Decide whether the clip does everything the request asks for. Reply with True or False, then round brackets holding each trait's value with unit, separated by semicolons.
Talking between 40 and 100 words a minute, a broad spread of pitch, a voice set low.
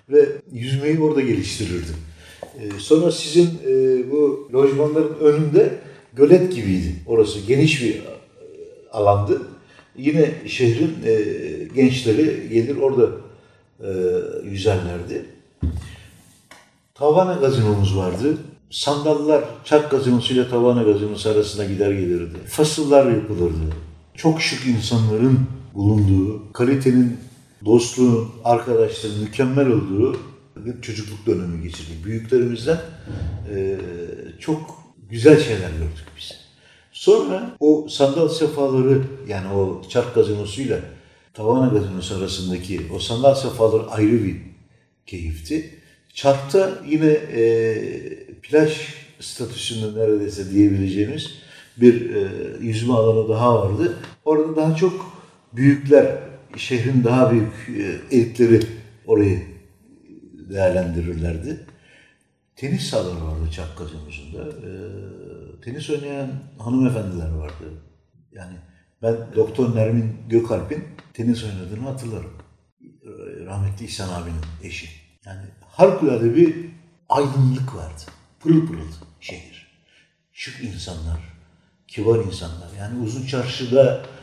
True (95 wpm; 7.1 semitones; 115 Hz)